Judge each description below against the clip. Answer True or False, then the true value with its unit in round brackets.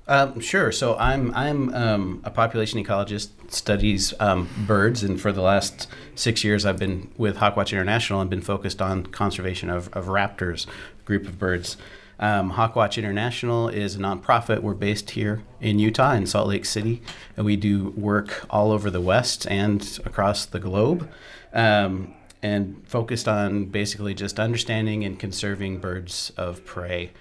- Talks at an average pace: True (165 wpm)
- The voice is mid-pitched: False (105 Hz)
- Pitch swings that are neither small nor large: False (2.1 semitones)